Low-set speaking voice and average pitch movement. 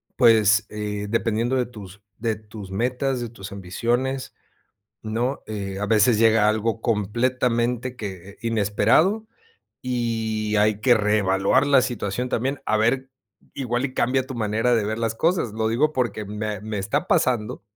Yes: low, 115 Hz; average, 3.0 semitones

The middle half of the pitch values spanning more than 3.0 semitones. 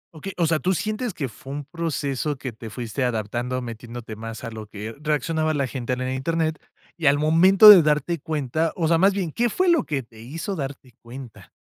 Yes: average, 5.2 semitones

